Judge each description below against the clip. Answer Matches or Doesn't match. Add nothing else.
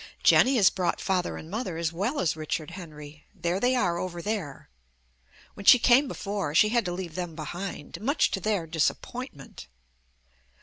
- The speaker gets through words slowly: Doesn't match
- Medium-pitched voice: Matches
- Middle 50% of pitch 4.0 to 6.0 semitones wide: Matches